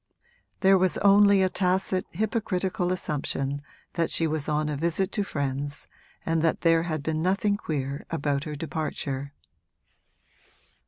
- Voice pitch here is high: No, medium, 165 Hz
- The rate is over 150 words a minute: No, average, 140 wpm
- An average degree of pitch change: Yes, average, 4.4 semitones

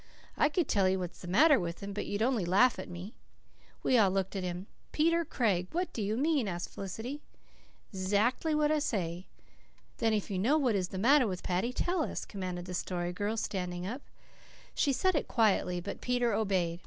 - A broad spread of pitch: Yes, wide, 5.9 semitones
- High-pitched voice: Yes, high, 205 Hz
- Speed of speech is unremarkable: No, fast, 210 wpm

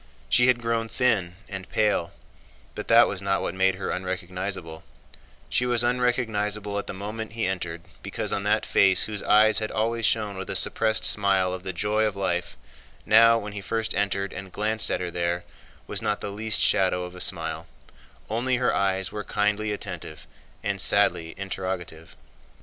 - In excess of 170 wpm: Yes, average, 180 wpm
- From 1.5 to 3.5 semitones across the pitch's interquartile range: Yes, average, 2.8 semitones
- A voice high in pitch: No, low, 100 Hz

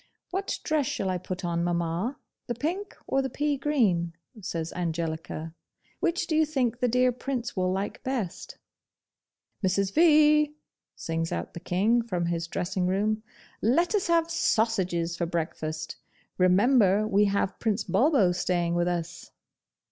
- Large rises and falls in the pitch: Yes, wide, 7.5 semitones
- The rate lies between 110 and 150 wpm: Yes, average, 145 wpm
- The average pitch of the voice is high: Yes, high, 200 Hz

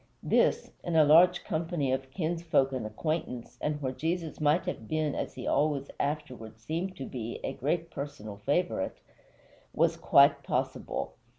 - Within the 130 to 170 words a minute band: Yes, average, 155 wpm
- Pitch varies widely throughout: No, average, 3.9 semitones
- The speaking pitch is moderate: Yes, medium, 150 Hz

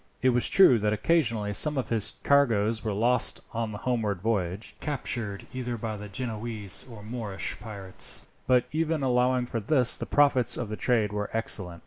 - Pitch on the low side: Yes, low, 115 Hz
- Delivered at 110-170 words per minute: No, average, 180 wpm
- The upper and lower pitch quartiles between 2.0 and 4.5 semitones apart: Yes, average, 3.3 semitones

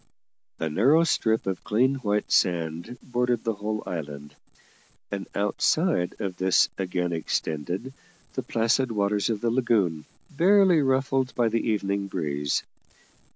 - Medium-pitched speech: No, low, 105 Hz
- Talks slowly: Yes, slow, 130 wpm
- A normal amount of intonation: No, wide, 5.7 semitones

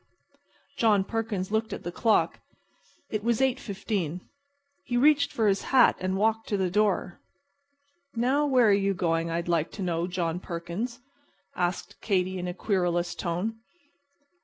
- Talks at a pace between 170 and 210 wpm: No, average, 150 wpm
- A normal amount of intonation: Yes, average, 4.2 semitones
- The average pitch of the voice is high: Yes, high, 195 Hz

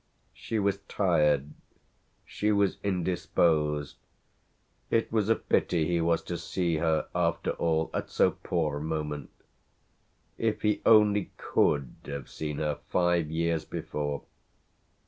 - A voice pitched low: Yes, very low, 85 Hz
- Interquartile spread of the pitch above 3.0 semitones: Yes, average, 4.5 semitones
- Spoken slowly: Yes, slow, 125 wpm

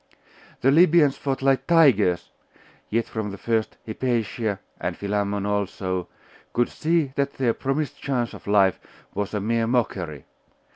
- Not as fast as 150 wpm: Yes, average, 140 wpm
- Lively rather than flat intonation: No, average, 5.0 semitones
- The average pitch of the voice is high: No, low, 115 Hz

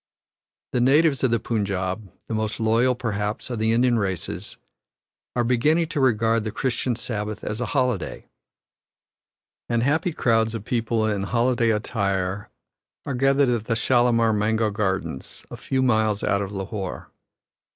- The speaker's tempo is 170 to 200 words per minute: No, average, 150 wpm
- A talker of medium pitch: No, low, 115 Hz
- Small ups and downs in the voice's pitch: No, average, 3.0 semitones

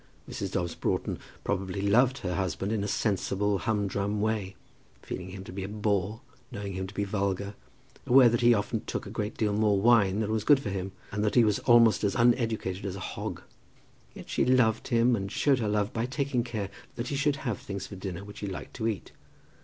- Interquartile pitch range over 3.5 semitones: No, average, 3.0 semitones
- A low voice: Yes, low, 105 Hz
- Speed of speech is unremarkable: No, fast, 215 wpm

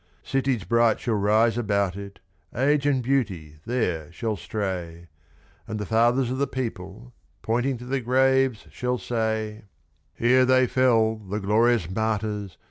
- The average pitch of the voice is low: Yes, low, 115 Hz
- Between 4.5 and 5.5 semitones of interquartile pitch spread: No, average, 3.7 semitones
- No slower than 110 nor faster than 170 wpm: Yes, average, 140 wpm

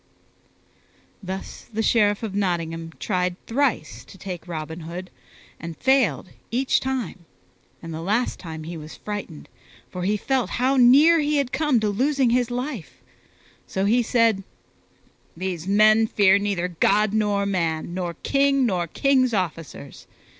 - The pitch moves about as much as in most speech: No, wide, 5.9 semitones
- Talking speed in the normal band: Yes, average, 145 wpm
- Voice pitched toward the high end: Yes, high, 205 Hz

